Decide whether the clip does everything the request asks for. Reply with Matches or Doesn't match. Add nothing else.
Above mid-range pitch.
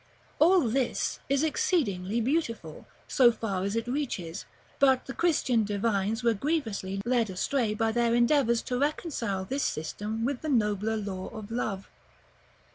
Matches